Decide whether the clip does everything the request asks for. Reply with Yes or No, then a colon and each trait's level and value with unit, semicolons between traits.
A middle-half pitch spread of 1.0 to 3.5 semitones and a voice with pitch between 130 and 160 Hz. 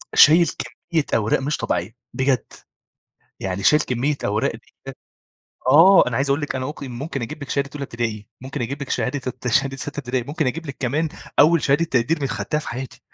Yes: average, 3.2 semitones; low, 135 Hz